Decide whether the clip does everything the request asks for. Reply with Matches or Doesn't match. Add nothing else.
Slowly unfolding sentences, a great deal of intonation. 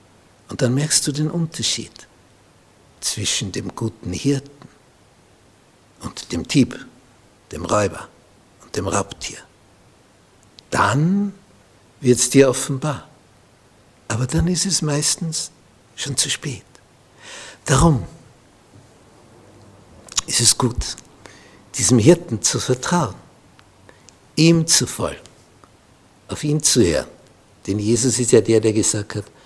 Matches